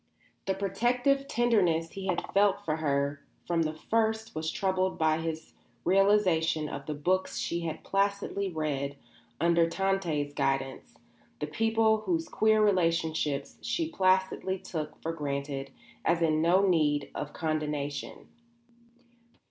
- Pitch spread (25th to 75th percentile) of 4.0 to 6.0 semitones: Yes, average, 4.3 semitones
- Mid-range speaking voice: Yes, medium, 170 Hz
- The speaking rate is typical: No, slow, 130 wpm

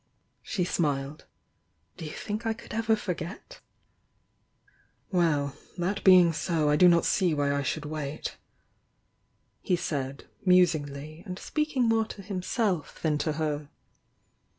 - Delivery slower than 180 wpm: Yes, average, 140 wpm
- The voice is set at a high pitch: No, medium, 170 Hz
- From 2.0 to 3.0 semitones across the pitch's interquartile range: No, average, 4.5 semitones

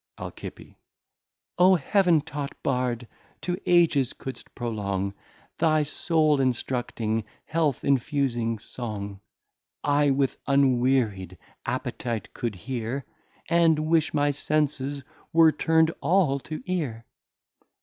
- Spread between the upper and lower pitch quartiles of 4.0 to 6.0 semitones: Yes, average, 4.5 semitones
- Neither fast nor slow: No, slow, 100 wpm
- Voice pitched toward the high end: No, medium, 140 Hz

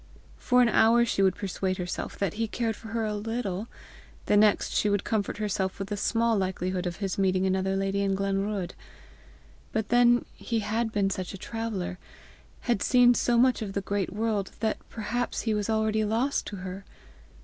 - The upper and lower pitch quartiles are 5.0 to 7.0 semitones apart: No, average, 2.7 semitones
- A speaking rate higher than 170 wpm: Yes, average, 190 wpm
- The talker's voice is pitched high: Yes, high, 210 Hz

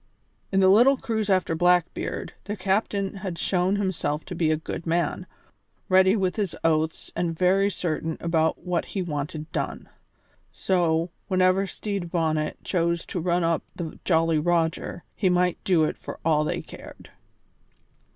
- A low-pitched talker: No, medium, 175 Hz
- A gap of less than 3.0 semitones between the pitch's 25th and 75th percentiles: Yes, narrow, 2.6 semitones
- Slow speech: No, average, 160 wpm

